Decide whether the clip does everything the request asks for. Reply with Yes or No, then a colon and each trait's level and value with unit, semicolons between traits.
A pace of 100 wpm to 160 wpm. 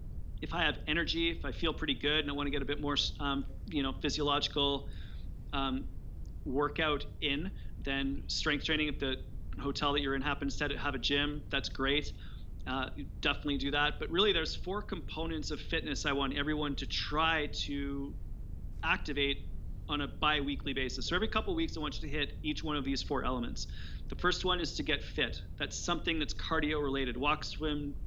No: average, 200 wpm